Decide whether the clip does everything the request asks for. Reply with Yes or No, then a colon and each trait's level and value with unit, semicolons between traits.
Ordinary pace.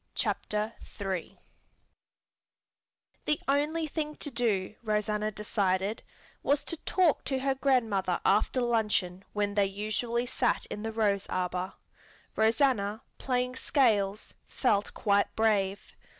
No: slow, 115 wpm